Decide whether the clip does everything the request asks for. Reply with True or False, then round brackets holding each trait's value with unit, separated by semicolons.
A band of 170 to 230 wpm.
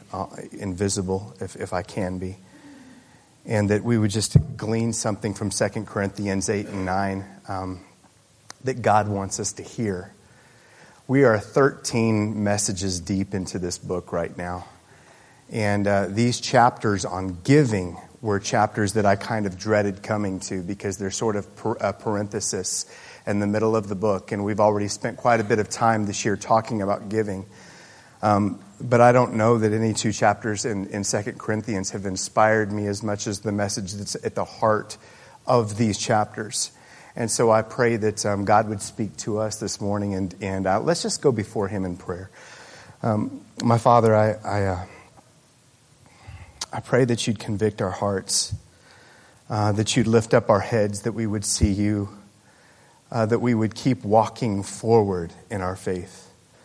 True (180 wpm)